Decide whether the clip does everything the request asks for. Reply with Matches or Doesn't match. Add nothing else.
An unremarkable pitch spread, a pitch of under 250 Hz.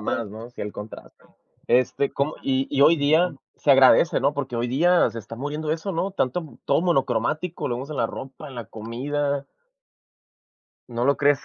Matches